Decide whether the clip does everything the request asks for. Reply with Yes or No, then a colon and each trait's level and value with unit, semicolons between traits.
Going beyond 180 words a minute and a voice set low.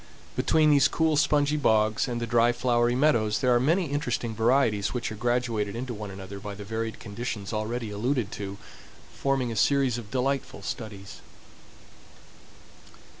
No: average, 155 wpm; low, 120 Hz